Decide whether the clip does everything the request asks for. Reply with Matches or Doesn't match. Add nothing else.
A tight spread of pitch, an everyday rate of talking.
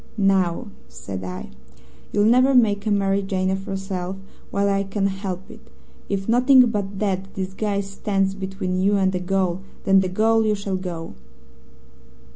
Matches